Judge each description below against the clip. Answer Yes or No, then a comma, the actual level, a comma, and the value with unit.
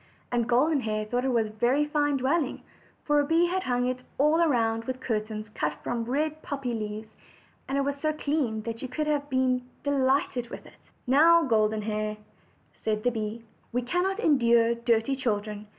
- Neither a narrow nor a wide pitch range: Yes, average, 4.3 semitones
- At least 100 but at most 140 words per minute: No, average, 190 wpm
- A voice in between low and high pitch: No, very high, 250 Hz